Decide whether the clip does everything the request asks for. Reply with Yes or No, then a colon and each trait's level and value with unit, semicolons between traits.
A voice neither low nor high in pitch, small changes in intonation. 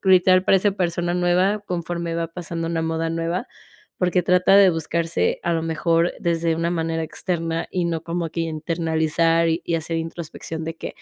Yes: medium, 165 Hz; narrow, 1.3 semitones